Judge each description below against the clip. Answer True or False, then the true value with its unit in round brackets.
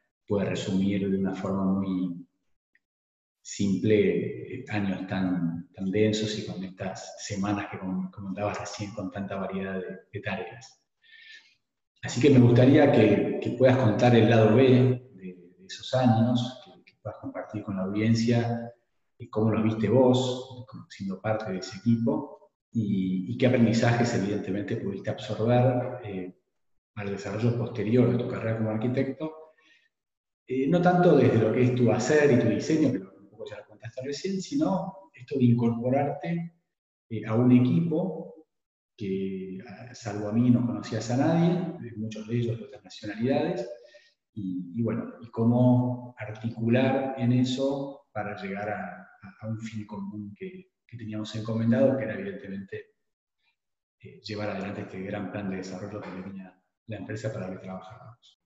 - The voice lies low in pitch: True (110 Hz)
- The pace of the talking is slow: False (160 wpm)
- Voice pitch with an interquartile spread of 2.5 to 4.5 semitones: True (3.9 semitones)